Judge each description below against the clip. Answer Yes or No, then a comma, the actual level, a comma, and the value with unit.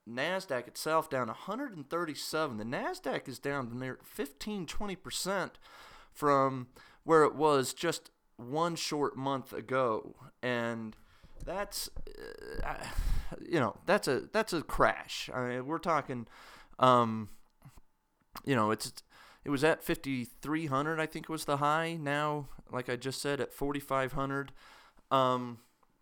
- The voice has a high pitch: No, medium, 140 Hz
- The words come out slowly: Yes, slow, 130 wpm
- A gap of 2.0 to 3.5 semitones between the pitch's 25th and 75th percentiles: No, average, 4.2 semitones